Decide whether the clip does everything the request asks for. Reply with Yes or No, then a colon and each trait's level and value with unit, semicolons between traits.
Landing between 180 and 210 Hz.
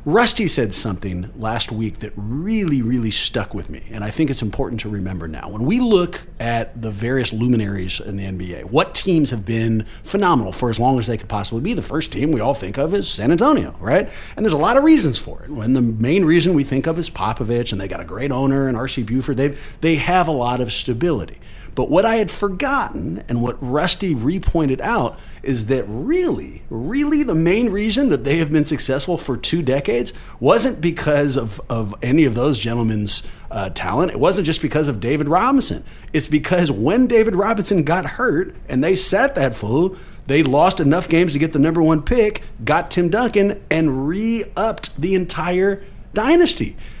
No: medium, 140 Hz